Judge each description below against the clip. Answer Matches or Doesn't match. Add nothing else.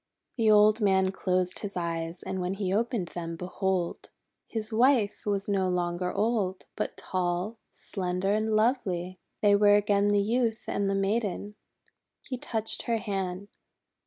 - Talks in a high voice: Matches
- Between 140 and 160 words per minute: Matches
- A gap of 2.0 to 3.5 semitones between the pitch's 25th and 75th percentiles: Matches